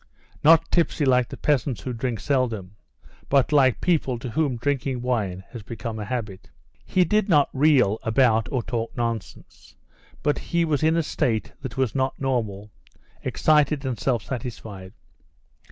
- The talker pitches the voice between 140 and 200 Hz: No, low, 125 Hz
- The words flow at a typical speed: Yes, average, 155 wpm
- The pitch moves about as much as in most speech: Yes, average, 4.2 semitones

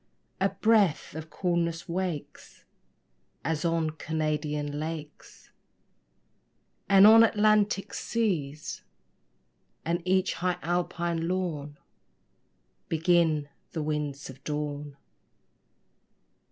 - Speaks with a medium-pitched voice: Yes, medium, 165 Hz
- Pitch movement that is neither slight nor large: Yes, average, 3.4 semitones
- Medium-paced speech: No, slow, 85 wpm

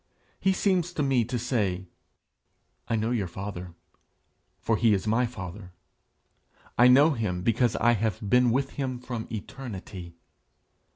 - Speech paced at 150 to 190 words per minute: No, average, 140 wpm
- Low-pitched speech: Yes, low, 115 Hz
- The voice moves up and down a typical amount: Yes, average, 4.1 semitones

